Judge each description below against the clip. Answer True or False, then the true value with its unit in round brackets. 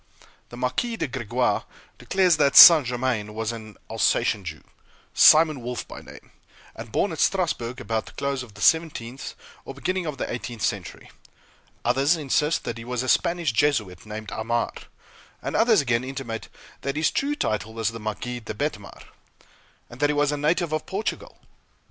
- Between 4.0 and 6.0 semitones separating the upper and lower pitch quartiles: True (5.1 semitones)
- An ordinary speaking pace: True (175 wpm)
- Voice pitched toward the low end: True (130 Hz)